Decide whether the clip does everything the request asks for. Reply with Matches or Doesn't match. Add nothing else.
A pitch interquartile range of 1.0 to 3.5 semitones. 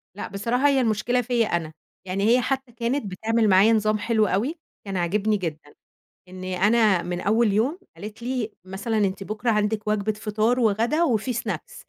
Matches